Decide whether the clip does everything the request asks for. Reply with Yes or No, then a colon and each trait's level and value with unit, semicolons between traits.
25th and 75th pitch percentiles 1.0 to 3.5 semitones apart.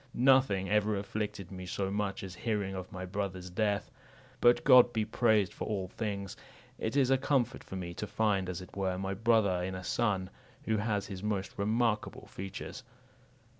Yes: average, 2.7 semitones